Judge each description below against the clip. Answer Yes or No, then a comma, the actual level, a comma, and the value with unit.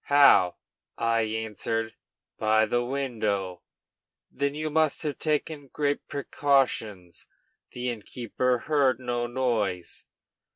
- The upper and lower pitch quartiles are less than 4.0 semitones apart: No, average, 4.4 semitones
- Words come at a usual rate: No, slow, 100 wpm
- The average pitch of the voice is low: Yes, low, 120 Hz